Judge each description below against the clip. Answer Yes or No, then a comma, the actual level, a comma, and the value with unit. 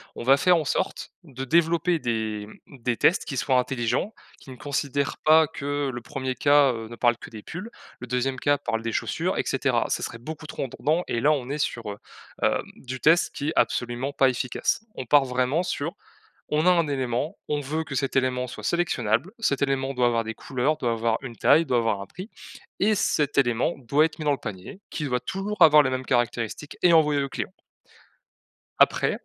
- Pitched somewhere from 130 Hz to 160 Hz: Yes, low, 135 Hz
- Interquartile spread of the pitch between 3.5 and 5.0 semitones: Yes, average, 4.0 semitones